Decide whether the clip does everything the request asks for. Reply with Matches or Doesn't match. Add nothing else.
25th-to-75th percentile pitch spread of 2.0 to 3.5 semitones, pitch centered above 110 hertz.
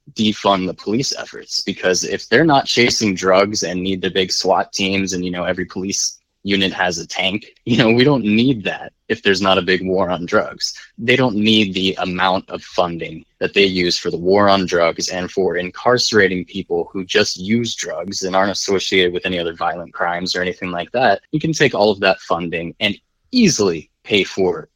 Doesn't match